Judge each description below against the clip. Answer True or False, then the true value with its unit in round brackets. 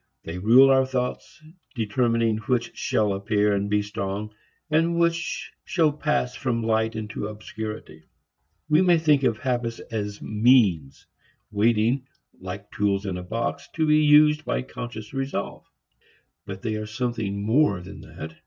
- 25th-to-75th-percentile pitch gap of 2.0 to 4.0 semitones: False (4.4 semitones)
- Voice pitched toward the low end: True (110 Hz)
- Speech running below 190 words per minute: True (145 wpm)